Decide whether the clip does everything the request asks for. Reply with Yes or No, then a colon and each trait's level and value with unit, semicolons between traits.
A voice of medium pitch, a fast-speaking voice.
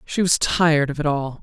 Yes: medium, 150 Hz; fast, 255 wpm